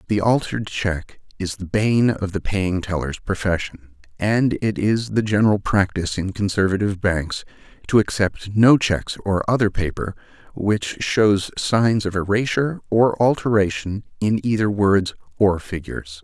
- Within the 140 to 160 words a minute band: Yes, average, 145 wpm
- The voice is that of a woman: No, male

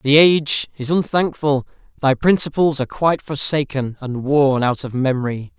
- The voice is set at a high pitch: No, medium, 140 Hz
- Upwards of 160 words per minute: No, average, 150 wpm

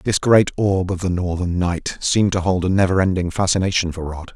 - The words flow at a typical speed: No, fast, 220 wpm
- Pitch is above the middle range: No, very low, 90 Hz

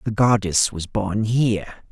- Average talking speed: Yes, average, 155 wpm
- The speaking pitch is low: Yes, low, 105 Hz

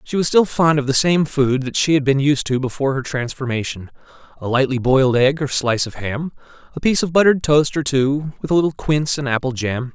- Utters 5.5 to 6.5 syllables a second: Yes, 6.0 syllables/s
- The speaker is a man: Yes, male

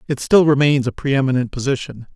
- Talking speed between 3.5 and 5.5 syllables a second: No, 6.5 syllables/s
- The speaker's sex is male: Yes, male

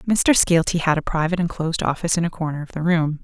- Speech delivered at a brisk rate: Yes, fast, 240 wpm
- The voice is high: No, medium, 165 Hz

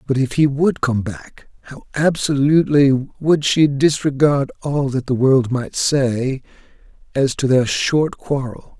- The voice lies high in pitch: No, low, 135 Hz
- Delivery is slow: No, average, 150 wpm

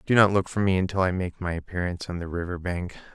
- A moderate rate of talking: No, fast, 265 wpm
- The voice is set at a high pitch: No, very low, 90 Hz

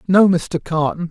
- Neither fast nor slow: Yes, average, 160 wpm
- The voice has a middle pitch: Yes, medium, 170 Hz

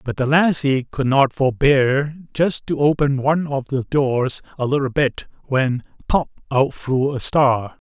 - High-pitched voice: No, low, 135 Hz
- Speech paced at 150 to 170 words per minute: Yes, average, 160 wpm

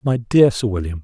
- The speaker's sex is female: No, male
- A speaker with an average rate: No, fast, 235 wpm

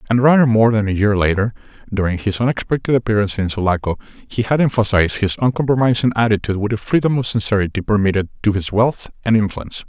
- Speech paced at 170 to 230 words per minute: Yes, average, 180 wpm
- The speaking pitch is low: Yes, low, 110 Hz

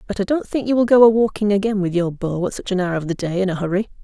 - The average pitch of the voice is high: Yes, high, 200 Hz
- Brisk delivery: Yes, fast, 340 wpm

